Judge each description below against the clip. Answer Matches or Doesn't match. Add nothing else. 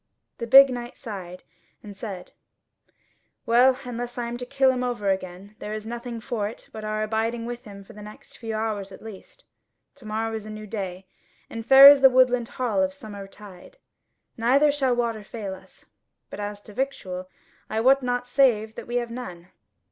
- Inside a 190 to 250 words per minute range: Matches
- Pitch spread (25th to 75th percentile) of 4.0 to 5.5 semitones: Doesn't match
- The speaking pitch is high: Matches